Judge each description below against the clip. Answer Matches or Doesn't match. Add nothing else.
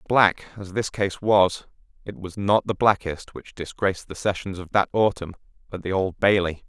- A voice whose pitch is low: Matches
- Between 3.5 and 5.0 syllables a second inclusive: Matches